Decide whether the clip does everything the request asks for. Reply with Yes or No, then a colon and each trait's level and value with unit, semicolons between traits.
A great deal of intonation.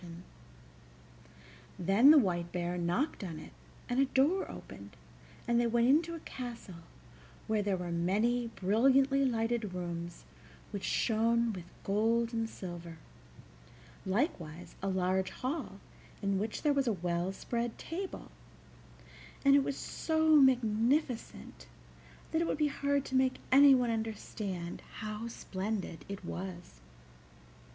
Yes: wide, 6.3 semitones